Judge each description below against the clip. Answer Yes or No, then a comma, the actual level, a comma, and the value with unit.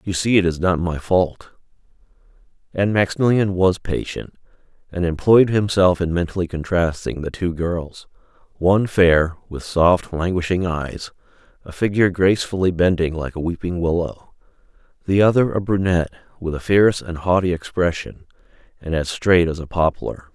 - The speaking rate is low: No, average, 145 wpm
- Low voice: Yes, very low, 90 Hz